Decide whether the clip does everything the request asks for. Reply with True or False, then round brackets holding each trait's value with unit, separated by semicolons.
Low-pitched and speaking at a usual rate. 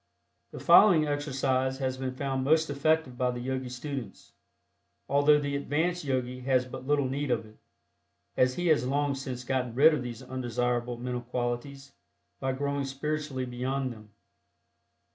True (130 Hz; 155 wpm)